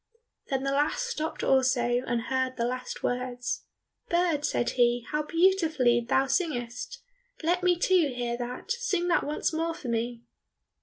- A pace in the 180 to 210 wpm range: No, average, 155 wpm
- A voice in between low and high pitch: No, very high, 265 Hz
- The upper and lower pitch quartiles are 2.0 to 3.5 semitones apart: No, average, 5.3 semitones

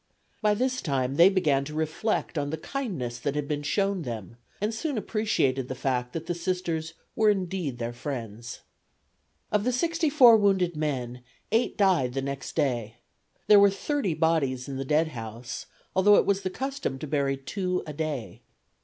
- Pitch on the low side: No, medium, 160 Hz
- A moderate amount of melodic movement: No, wide, 7.1 semitones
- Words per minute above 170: Yes, average, 180 wpm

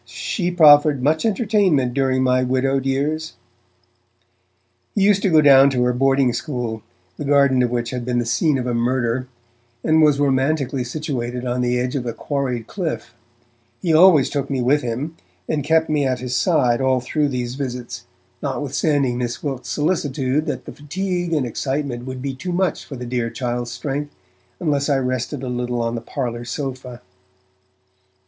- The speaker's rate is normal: Yes, average, 175 wpm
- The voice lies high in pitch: No, low, 135 Hz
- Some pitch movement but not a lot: Yes, average, 3.2 semitones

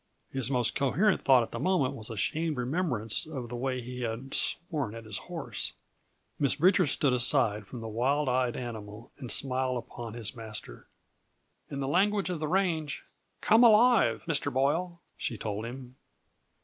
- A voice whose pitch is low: Yes, low, 130 Hz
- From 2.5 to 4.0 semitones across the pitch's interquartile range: No, average, 5.2 semitones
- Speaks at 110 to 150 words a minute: No, average, 170 wpm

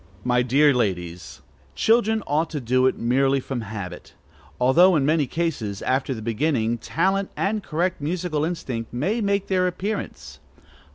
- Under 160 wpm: Yes, average, 150 wpm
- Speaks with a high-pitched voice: No, medium, 145 Hz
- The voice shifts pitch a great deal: Yes, wide, 6.9 semitones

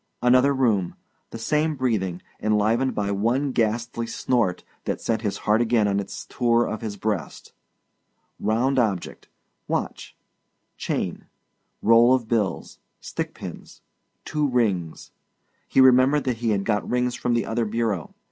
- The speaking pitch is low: Yes, low, 115 Hz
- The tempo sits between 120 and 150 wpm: Yes, average, 140 wpm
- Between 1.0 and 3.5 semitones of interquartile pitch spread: Yes, average, 3.1 semitones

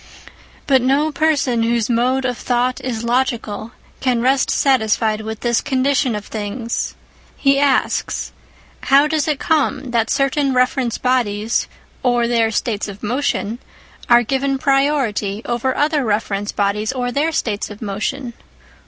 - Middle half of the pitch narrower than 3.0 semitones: No, average, 3.6 semitones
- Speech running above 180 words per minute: No, average, 145 wpm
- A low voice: No, high, 245 Hz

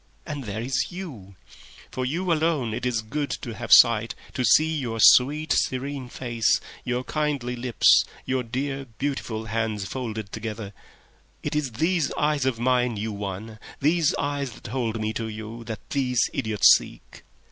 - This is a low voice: Yes, low, 125 Hz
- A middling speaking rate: Yes, average, 160 wpm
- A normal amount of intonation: Yes, average, 4.1 semitones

